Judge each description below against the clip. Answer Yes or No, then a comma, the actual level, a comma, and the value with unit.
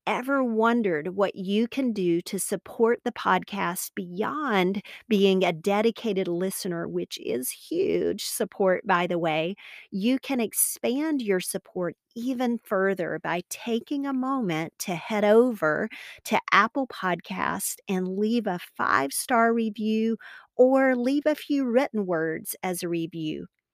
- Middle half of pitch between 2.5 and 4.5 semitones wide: No, average, 5.1 semitones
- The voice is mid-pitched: No, high, 210 Hz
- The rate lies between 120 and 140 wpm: Yes, slow, 135 wpm